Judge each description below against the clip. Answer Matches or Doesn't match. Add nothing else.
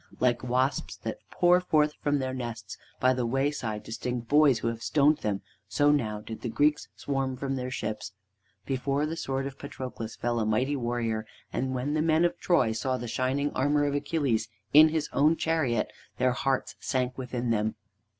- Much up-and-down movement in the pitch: Doesn't match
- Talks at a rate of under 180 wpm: Doesn't match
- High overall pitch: Doesn't match